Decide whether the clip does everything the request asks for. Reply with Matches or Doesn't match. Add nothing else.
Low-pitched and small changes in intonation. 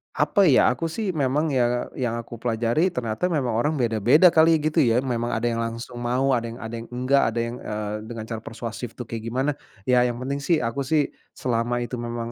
Doesn't match